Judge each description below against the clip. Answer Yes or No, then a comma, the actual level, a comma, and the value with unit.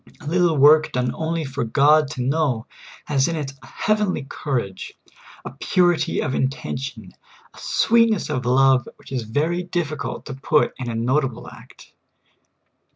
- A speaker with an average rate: Yes, average, 160 wpm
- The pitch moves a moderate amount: Yes, average, 3.9 semitones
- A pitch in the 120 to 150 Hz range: Yes, medium, 140 Hz